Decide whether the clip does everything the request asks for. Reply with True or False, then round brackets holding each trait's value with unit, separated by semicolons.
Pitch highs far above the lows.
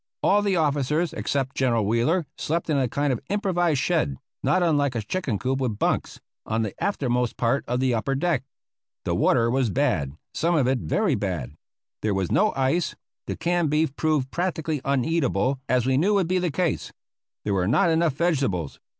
True (5.8 semitones)